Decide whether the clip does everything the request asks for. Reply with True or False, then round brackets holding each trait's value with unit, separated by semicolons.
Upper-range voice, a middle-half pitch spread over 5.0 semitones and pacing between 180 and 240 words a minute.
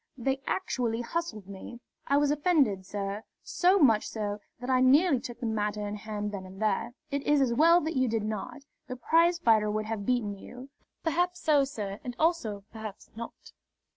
True (240 Hz; 5.4 semitones; 185 wpm)